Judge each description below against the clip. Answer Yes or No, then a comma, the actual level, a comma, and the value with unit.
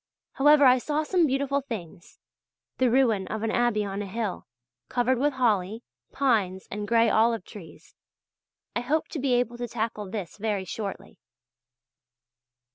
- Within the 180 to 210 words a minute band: No, average, 150 wpm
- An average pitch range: Yes, average, 4.0 semitones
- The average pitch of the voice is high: Yes, high, 230 Hz